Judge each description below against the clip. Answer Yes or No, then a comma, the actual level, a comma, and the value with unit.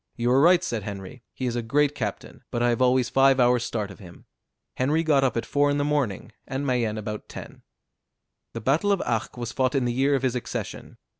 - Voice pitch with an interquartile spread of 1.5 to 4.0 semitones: Yes, average, 3.2 semitones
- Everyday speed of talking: No, fast, 230 wpm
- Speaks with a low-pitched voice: Yes, low, 125 Hz